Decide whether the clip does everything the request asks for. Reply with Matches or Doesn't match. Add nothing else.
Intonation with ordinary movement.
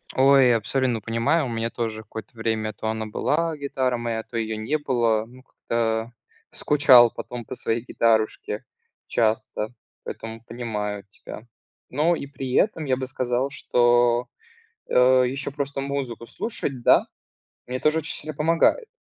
Matches